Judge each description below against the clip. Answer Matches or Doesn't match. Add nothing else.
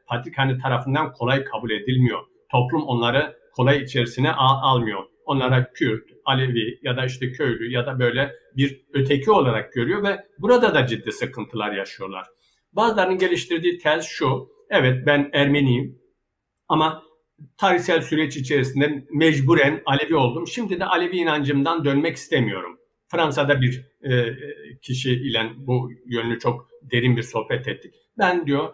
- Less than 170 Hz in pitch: Matches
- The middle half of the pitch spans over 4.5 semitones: Doesn't match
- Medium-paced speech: Matches